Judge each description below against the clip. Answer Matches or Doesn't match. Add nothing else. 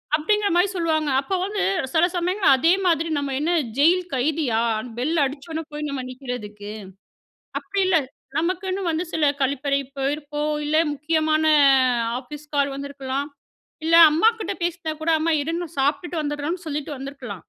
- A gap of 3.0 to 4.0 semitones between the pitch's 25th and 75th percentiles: Matches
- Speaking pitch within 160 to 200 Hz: Doesn't match